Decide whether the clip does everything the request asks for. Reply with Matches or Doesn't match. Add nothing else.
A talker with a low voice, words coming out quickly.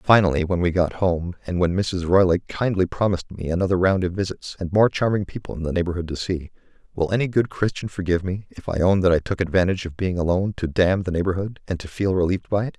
Matches